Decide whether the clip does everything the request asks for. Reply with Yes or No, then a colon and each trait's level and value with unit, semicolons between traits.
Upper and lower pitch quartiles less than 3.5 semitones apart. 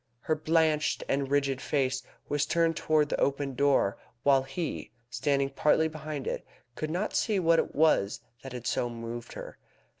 Yes: average, 2.8 semitones